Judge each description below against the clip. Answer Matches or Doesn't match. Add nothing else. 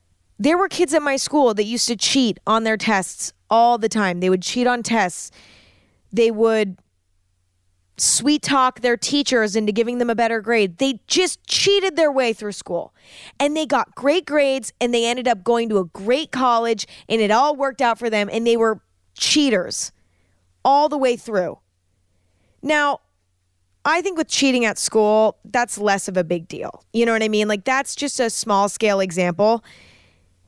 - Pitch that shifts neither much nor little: Doesn't match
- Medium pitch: Doesn't match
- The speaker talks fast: Doesn't match